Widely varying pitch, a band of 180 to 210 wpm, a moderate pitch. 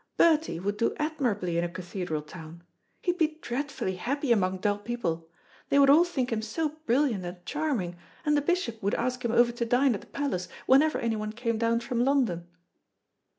No: wide, 6.9 semitones; average, 190 wpm; high, 235 Hz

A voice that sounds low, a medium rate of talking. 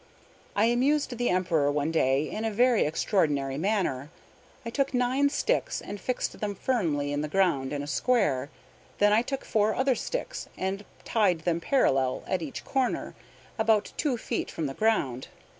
No: high, 200 Hz; average, 170 wpm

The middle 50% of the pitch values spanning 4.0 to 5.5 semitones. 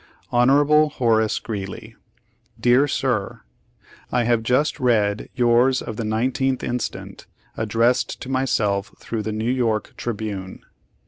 No: average, 2.9 semitones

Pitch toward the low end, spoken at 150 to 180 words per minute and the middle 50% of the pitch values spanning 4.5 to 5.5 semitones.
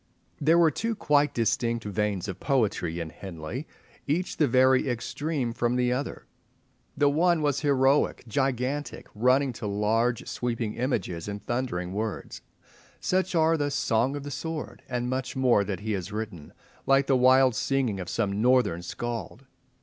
Yes: low, 125 Hz; average, 155 wpm; average, 4.9 semitones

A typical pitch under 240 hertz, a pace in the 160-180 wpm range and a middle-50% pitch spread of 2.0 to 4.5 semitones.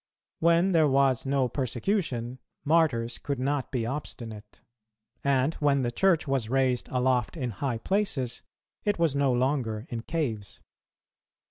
No: low, 135 Hz; slow, 135 wpm; average, 3.6 semitones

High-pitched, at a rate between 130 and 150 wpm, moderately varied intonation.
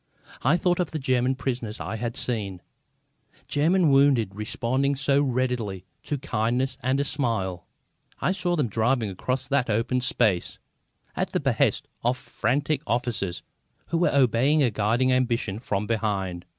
No: low, 125 Hz; average, 145 wpm; average, 4.0 semitones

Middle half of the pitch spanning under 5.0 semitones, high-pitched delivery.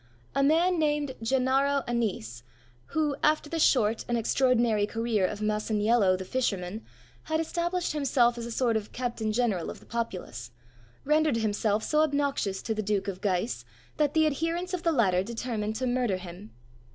No: wide, 5.4 semitones; high, 235 Hz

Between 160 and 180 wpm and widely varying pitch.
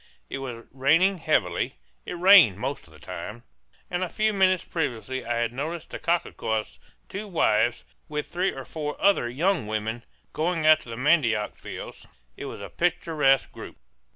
Yes: average, 170 wpm; wide, 7.0 semitones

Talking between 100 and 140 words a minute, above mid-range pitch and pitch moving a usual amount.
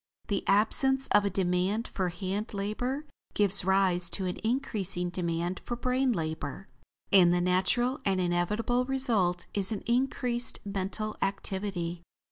Yes: slow, 135 wpm; high, 195 Hz; average, 4.5 semitones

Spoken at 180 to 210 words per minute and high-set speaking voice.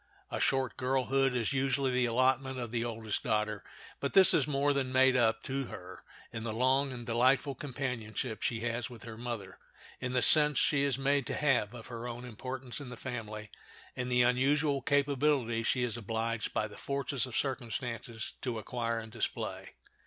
No: average, 185 wpm; low, 125 Hz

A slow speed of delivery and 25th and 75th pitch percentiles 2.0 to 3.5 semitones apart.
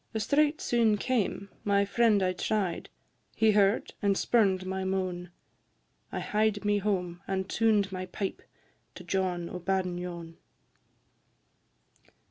Yes: slow, 125 wpm; narrow, 2.4 semitones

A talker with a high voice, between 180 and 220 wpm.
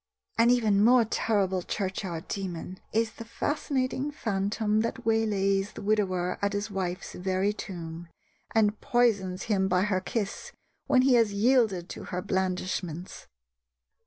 No: high, 200 Hz; slow, 135 wpm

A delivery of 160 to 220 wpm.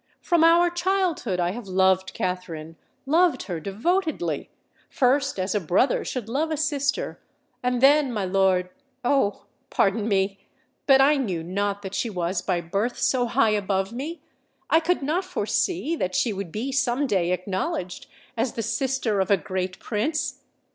No: average, 145 wpm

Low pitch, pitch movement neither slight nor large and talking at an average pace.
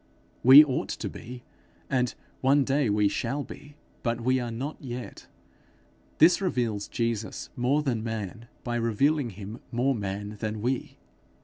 Yes: low, 120 Hz; average, 3.5 semitones; average, 145 wpm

